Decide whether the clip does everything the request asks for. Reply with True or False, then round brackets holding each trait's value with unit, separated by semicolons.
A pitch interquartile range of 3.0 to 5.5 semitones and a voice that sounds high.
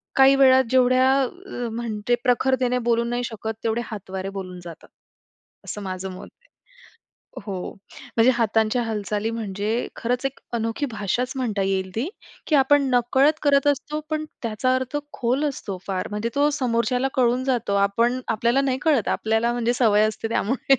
True (3.4 semitones; 235 Hz)